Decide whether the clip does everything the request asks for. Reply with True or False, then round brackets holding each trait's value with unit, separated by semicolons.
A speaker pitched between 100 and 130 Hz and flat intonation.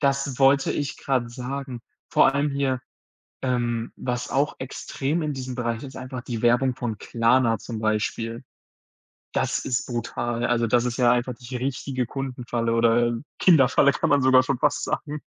True (125 Hz; 2.3 semitones)